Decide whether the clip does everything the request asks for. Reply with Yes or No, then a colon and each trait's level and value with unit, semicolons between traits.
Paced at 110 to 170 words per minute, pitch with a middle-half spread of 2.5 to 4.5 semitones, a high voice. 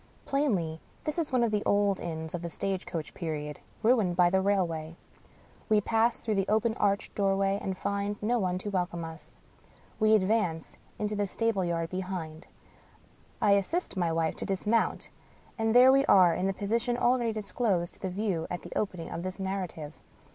No: average, 185 wpm; average, 3.8 semitones; high, 195 Hz